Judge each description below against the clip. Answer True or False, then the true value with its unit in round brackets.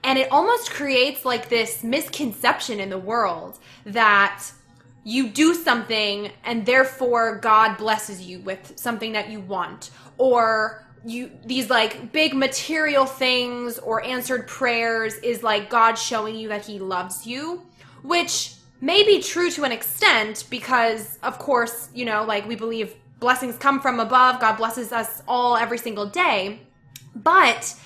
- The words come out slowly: False (150 wpm)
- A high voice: True (235 Hz)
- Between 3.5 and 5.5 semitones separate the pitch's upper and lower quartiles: False (3.0 semitones)